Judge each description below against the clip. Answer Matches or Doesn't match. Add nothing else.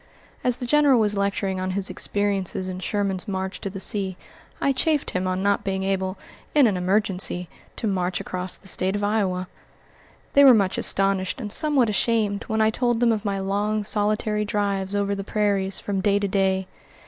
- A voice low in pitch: Doesn't match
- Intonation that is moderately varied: Doesn't match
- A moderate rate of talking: Matches